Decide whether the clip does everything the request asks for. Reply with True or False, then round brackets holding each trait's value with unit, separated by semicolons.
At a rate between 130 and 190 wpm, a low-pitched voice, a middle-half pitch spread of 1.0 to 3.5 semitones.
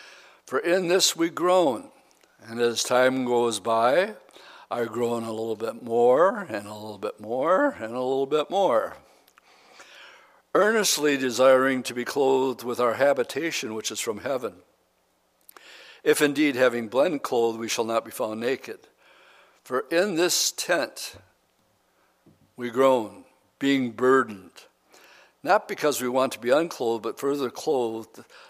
False (140 wpm; 130 Hz; 4.1 semitones)